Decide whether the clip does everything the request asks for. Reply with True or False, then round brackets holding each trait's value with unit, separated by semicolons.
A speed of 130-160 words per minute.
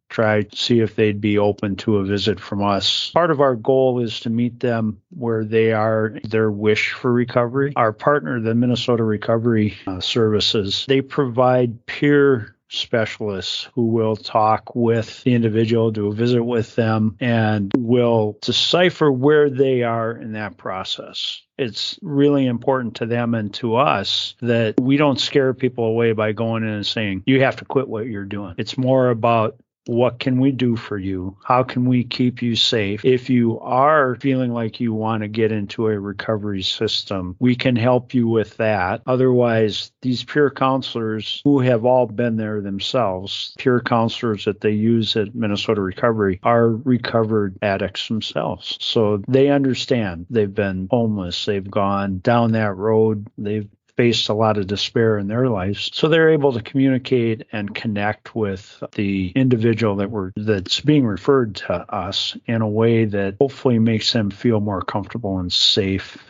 False (170 wpm)